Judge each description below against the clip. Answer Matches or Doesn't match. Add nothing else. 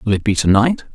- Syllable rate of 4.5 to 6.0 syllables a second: Matches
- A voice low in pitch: Matches